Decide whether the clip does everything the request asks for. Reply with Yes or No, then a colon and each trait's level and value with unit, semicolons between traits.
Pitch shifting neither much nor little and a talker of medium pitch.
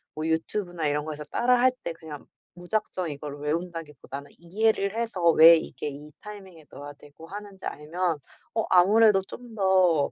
Yes: average, 5.0 semitones; medium, 170 Hz